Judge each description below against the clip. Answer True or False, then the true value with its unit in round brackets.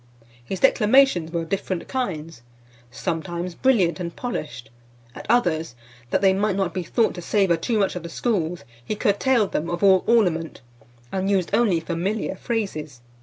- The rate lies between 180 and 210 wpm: False (165 wpm)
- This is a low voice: False (185 Hz)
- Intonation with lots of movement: False (4.1 semitones)